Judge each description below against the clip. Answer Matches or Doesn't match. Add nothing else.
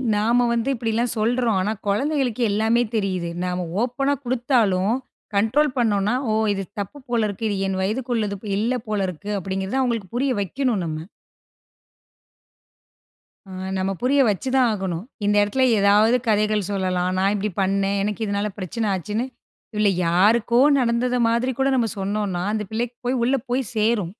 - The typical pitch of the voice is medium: Doesn't match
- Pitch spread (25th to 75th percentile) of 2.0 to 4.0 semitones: Matches